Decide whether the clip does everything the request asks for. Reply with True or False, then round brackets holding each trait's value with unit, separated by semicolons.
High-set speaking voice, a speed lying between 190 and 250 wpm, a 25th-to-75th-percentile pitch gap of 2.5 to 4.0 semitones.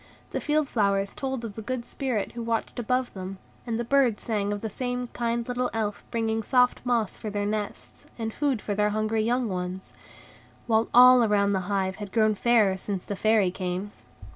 True (220 Hz; 195 wpm; 3.1 semitones)